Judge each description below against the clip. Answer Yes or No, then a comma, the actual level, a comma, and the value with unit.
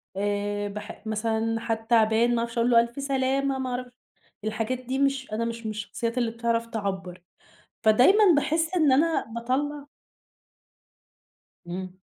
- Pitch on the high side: Yes, high, 230 Hz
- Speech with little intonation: No, average, 3.3 semitones